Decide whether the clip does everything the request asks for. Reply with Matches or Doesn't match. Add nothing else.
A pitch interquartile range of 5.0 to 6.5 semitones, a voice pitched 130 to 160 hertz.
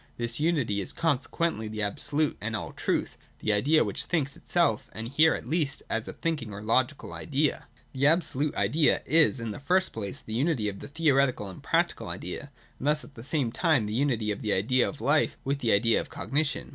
Matches